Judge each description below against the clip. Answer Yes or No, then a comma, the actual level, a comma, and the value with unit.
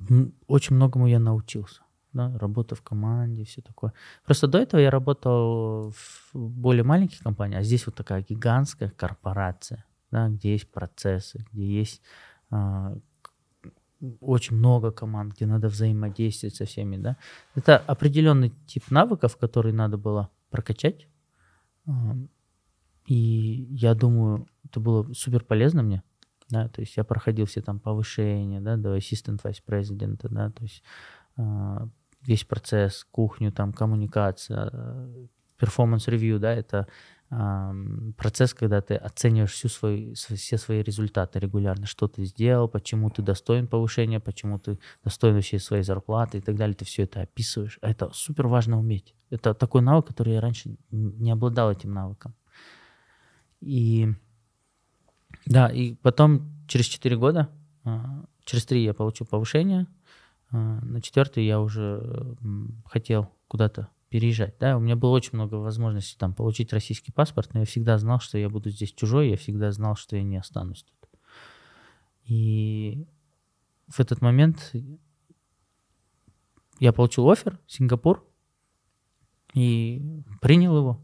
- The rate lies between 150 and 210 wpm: No, average, 135 wpm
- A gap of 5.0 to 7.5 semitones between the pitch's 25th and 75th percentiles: No, average, 3.2 semitones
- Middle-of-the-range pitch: No, low, 115 Hz